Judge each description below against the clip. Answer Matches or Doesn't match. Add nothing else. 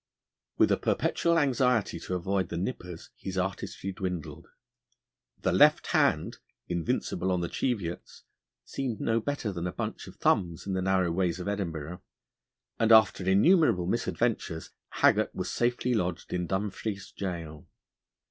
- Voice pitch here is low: Matches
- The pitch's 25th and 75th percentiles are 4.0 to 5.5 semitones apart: Matches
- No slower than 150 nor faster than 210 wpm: Doesn't match